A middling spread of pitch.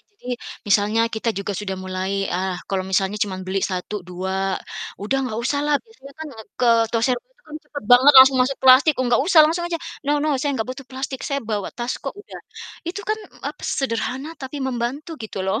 No: wide, 6.2 semitones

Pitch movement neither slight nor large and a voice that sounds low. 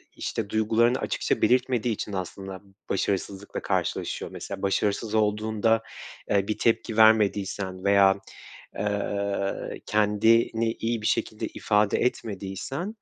No: narrow, 2.2 semitones; low, 105 Hz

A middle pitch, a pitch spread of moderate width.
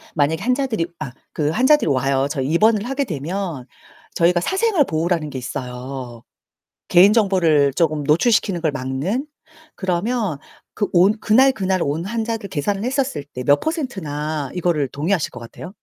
No: medium, 170 Hz; wide, 6.8 semitones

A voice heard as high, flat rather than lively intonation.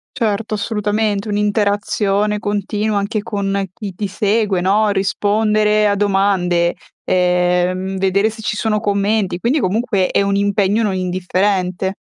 Yes: high, 205 Hz; narrow, 1.8 semitones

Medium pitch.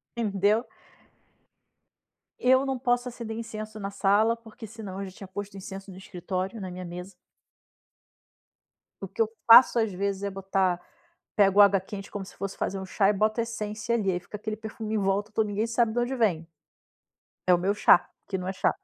No: high, 205 Hz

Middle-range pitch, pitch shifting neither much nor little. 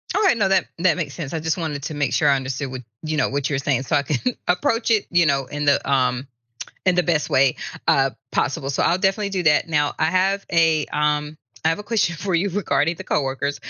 Yes: medium, 155 Hz; average, 4.5 semitones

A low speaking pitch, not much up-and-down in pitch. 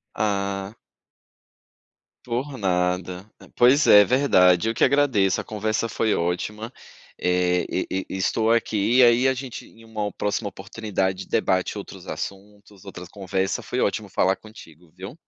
No: low, 100 Hz; average, 3.3 semitones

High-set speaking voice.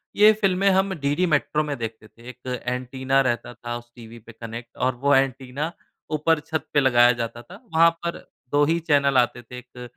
No: low, 130 Hz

